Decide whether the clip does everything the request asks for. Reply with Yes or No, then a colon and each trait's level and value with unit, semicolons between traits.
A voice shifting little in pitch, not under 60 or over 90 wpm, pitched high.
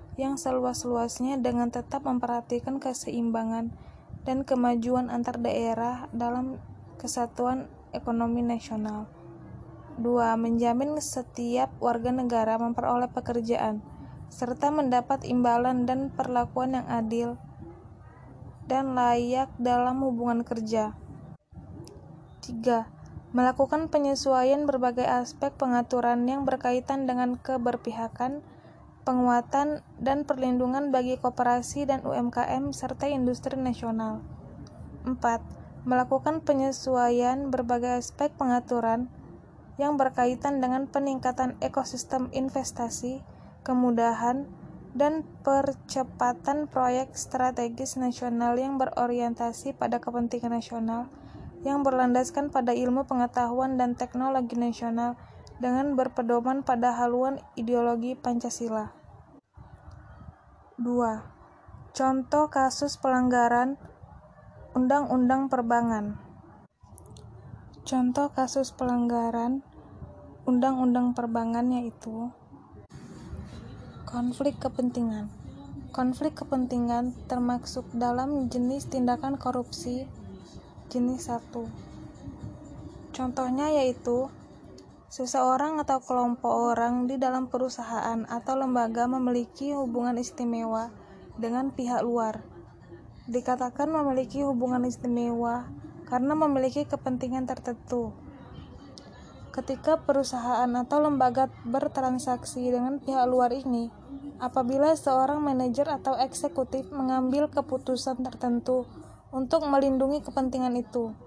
Yes: narrow, 1.7 semitones; slow, 85 wpm; very high, 250 Hz